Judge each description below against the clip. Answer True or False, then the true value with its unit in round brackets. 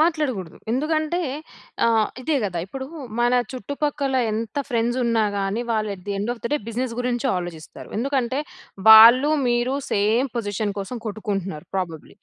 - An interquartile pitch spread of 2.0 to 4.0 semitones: False (4.4 semitones)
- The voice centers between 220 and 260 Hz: True (230 Hz)